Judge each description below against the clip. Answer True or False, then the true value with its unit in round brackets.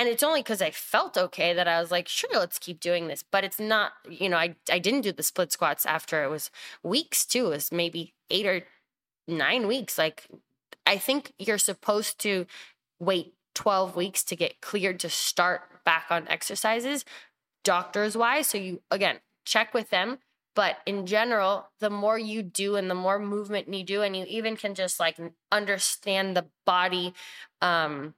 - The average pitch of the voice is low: False (195 Hz)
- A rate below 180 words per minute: False (185 wpm)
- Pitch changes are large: False (3.3 semitones)